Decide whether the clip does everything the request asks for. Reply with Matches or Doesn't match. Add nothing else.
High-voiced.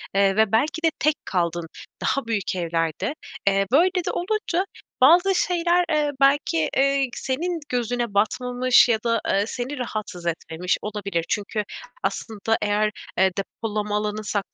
Matches